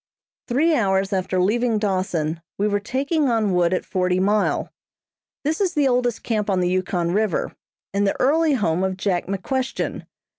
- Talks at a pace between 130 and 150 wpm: No, average, 165 wpm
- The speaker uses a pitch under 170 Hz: No, high, 205 Hz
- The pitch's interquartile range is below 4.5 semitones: No, average, 5.0 semitones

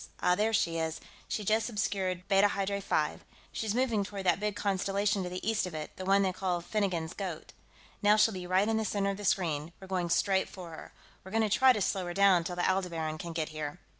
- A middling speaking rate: No, fast, 240 wpm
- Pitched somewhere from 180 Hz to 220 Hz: Yes, high, 190 Hz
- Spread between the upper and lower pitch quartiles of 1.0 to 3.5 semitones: Yes, average, 2.7 semitones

